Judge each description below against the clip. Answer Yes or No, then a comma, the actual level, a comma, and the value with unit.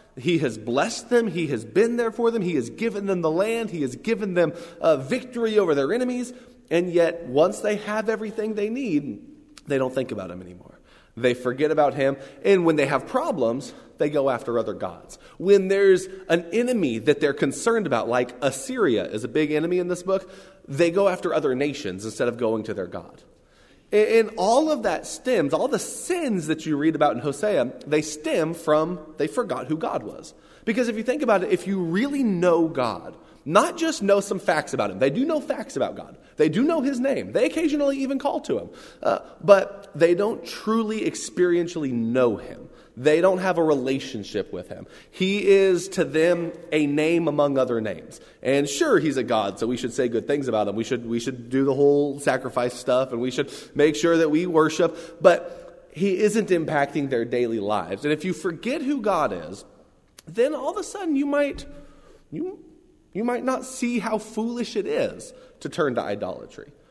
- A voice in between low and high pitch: Yes, medium, 180 Hz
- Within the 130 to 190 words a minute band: No, fast, 205 wpm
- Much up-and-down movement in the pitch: Yes, wide, 8.0 semitones